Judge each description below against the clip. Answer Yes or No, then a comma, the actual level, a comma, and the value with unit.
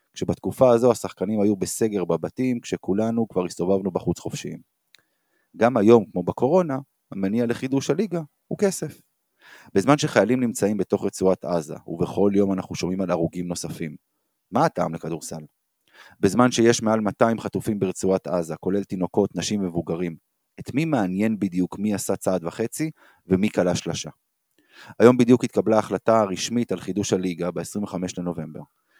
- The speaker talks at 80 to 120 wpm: No, average, 140 wpm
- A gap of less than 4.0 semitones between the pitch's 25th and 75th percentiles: No, average, 4.7 semitones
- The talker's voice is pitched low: Yes, low, 100 Hz